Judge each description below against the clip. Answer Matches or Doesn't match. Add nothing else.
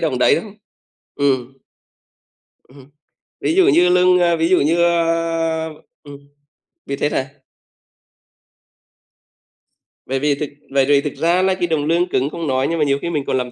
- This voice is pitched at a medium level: Matches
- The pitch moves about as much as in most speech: Matches